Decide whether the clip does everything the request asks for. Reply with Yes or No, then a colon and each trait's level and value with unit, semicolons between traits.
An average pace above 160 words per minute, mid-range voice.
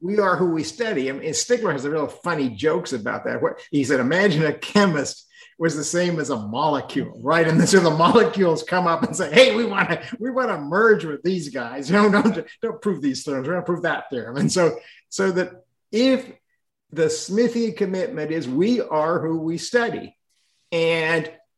Yes: fast, 205 wpm; medium, 175 Hz